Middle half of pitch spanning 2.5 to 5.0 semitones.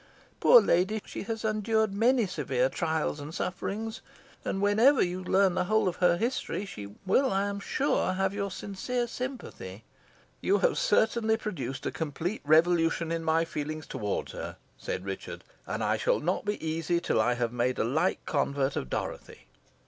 No: wide, 5.5 semitones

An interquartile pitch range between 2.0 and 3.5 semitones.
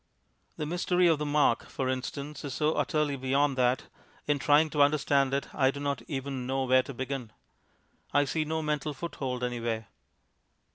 Yes: narrow, 2.5 semitones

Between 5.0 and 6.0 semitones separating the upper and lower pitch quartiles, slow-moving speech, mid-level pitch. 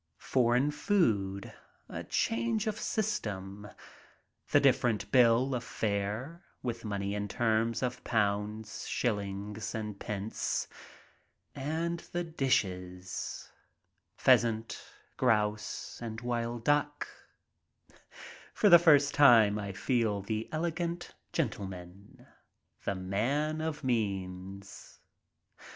No: wide, 5.6 semitones; slow, 105 wpm; low, 115 Hz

